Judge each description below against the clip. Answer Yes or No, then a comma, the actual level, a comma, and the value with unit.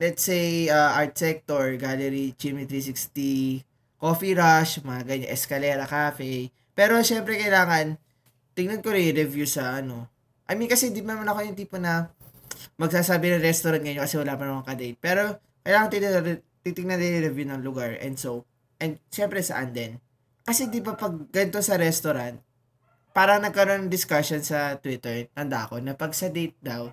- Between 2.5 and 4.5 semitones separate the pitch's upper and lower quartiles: No, wide, 5.5 semitones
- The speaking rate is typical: No, fast, 175 wpm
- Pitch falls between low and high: Yes, medium, 150 Hz